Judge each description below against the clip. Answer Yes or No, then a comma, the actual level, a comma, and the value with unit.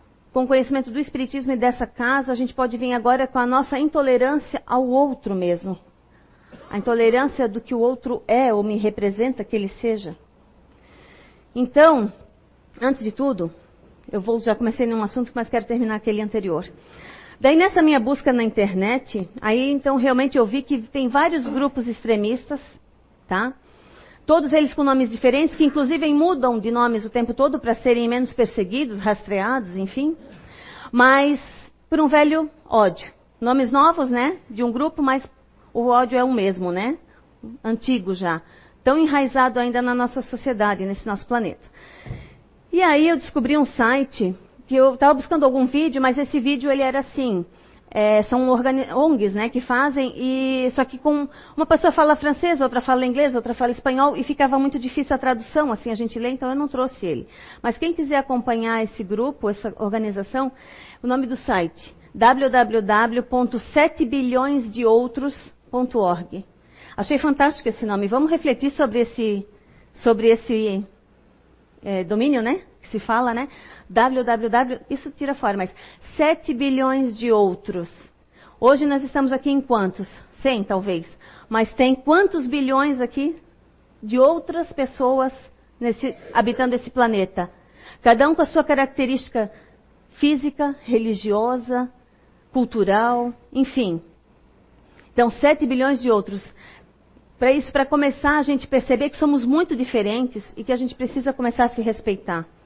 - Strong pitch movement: No, average, 3.5 semitones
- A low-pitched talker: No, very high, 255 Hz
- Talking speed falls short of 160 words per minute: Yes, average, 150 wpm